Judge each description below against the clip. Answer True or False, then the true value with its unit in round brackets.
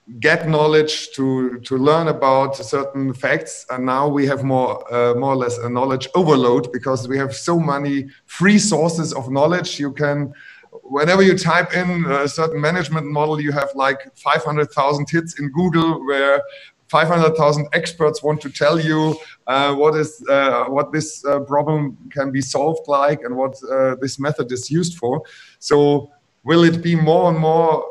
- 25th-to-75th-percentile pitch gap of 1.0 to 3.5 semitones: True (2.8 semitones)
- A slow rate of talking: False (180 wpm)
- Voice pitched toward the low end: False (145 Hz)